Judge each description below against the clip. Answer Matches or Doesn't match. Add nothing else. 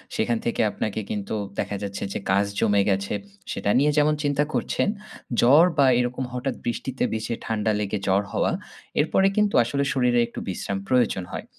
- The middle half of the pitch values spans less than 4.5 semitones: Doesn't match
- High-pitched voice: Doesn't match